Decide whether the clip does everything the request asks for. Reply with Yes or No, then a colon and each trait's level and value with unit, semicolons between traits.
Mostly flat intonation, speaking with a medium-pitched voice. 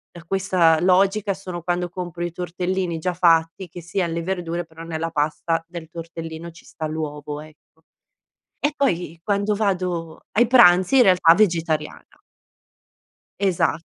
Yes: narrow, 2.3 semitones; medium, 175 Hz